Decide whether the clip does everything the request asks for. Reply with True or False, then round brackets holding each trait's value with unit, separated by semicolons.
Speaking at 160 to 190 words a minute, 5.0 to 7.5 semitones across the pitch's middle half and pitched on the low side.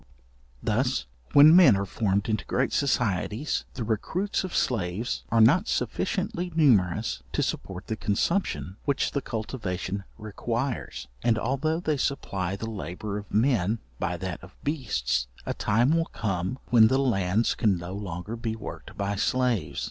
False (150 wpm; 5.5 semitones; 110 Hz)